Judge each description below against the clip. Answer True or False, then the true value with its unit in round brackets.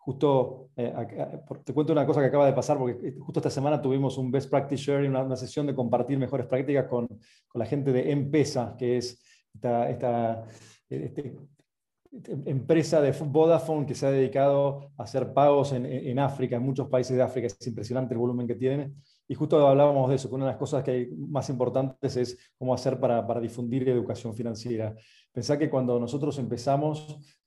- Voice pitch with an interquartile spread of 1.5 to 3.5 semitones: True (2.4 semitones)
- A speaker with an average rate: False (200 wpm)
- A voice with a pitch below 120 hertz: False (130 Hz)